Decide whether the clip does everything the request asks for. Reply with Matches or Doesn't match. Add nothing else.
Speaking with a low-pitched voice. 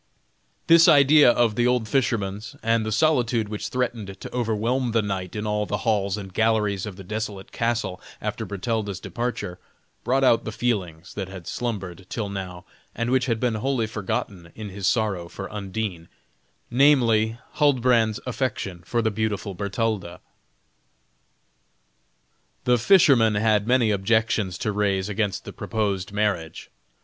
Matches